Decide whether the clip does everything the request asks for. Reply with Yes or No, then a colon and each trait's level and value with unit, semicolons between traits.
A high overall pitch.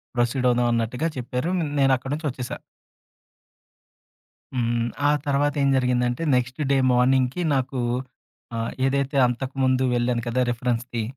No: low, 125 Hz